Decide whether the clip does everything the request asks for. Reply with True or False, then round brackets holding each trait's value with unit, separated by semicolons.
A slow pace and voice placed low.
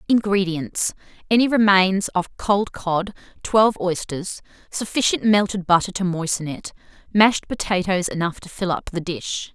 False (130 wpm; 190 Hz)